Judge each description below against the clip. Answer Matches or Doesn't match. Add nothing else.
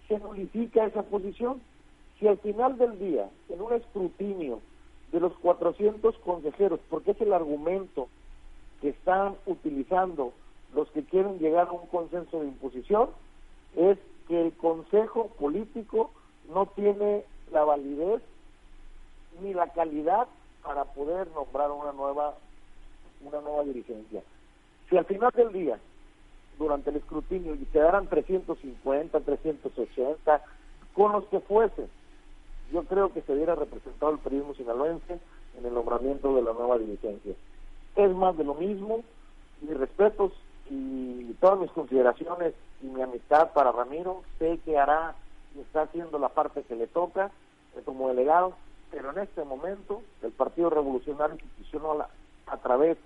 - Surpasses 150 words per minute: Doesn't match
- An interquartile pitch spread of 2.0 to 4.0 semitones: Doesn't match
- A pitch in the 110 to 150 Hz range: Doesn't match